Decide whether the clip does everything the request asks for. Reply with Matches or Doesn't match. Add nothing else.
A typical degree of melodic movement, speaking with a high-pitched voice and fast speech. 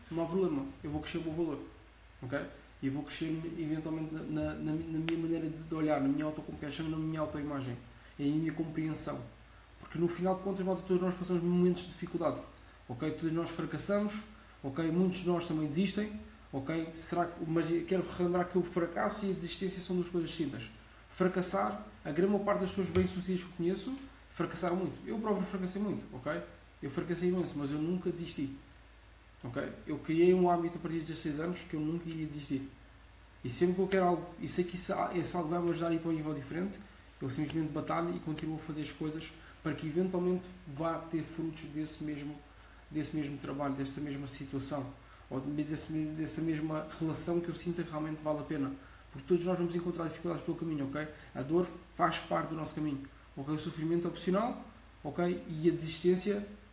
Doesn't match